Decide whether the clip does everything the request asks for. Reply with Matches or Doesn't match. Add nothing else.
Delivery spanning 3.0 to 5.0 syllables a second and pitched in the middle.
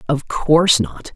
Matches